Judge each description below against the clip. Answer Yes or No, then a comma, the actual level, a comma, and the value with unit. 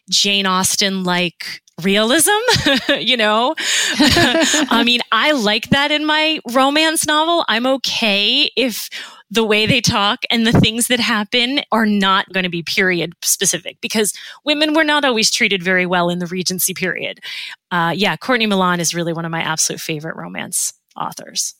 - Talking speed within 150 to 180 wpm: Yes, average, 165 wpm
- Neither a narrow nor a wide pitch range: No, wide, 6.1 semitones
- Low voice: No, high, 215 Hz